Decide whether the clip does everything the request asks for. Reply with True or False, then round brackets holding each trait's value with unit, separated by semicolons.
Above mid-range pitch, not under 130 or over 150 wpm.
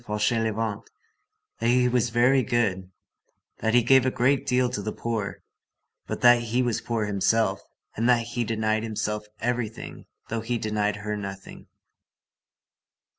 False (115 Hz; 145 wpm)